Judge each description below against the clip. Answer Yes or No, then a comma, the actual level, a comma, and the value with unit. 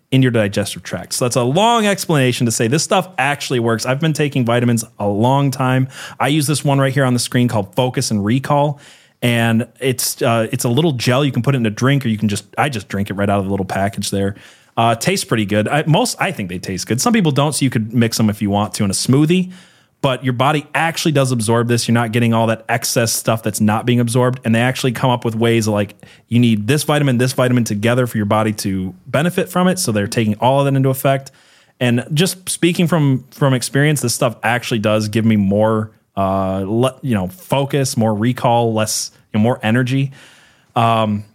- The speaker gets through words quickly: Yes, fast, 240 wpm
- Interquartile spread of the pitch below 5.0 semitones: Yes, average, 3.9 semitones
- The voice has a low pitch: Yes, low, 120 Hz